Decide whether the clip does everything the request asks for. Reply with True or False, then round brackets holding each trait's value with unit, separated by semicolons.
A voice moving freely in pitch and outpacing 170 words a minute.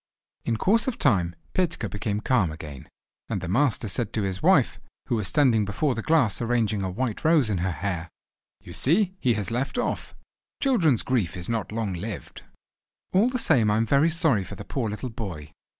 True (6.2 semitones; 195 wpm)